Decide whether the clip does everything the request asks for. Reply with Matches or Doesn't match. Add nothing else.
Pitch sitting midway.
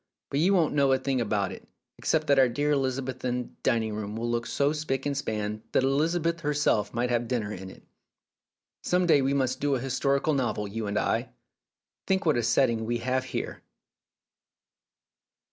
Doesn't match